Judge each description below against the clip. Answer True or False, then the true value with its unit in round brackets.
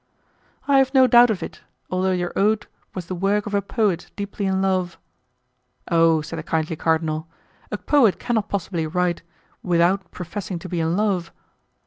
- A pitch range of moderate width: True (3.4 semitones)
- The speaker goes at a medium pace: True (170 wpm)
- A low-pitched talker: False (185 Hz)